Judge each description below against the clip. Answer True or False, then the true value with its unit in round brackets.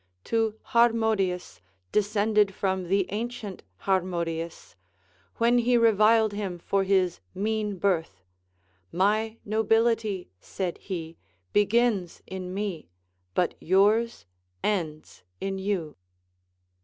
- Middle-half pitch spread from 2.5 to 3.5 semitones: True (3.2 semitones)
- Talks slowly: True (95 wpm)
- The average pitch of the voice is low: False (200 Hz)